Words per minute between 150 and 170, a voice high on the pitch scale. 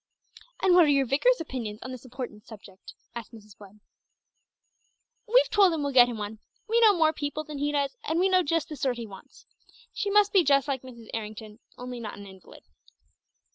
No: fast, 205 wpm; very high, 265 Hz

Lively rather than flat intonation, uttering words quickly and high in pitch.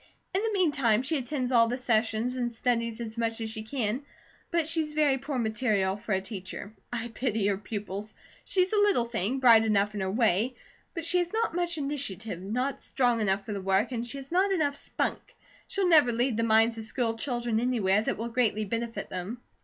No: average, 4.1 semitones; fast, 210 wpm; high, 235 Hz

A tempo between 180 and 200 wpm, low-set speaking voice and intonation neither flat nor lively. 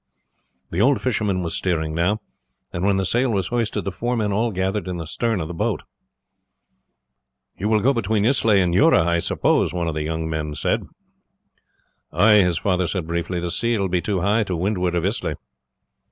Yes: average, 195 wpm; very low, 95 Hz; average, 3.9 semitones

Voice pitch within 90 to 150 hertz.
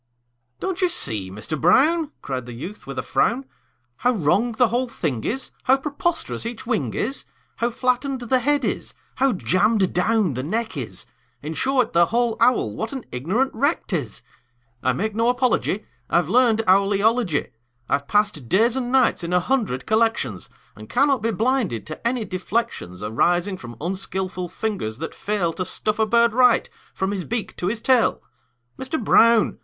No: high, 215 Hz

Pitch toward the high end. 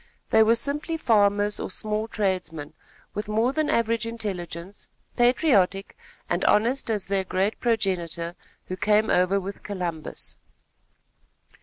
Yes: high, 205 Hz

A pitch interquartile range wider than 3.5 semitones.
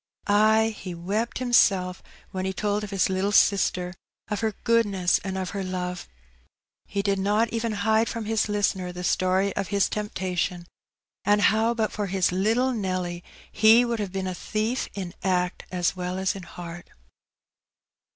No: average, 2.8 semitones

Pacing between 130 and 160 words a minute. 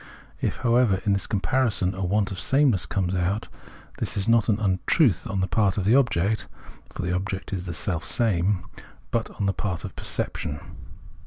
No: average, 185 wpm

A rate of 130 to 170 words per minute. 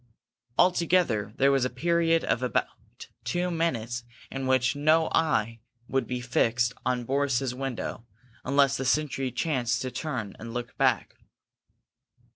Yes: slow, 135 wpm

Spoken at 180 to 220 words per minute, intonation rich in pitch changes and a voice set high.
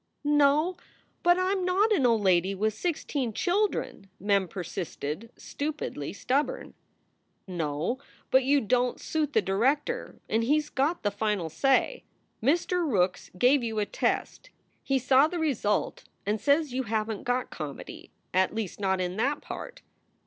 No: average, 155 wpm; wide, 6.9 semitones; very high, 250 Hz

